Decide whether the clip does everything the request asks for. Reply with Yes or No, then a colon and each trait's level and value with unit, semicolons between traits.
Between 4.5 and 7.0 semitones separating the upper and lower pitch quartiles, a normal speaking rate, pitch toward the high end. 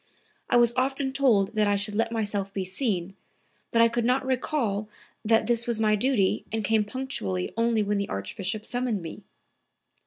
No: average, 3.2 semitones; average, 180 wpm; high, 220 Hz